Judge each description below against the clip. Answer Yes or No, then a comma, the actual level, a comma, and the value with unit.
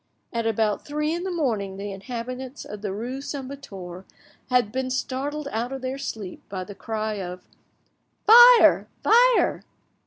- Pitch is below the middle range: No, very high, 250 Hz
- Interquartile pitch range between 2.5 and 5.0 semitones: No, wide, 5.4 semitones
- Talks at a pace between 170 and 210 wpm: No, average, 155 wpm